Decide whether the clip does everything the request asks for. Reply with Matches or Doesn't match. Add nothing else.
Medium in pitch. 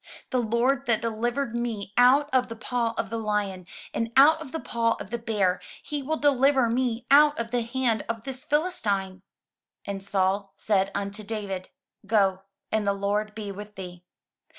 Doesn't match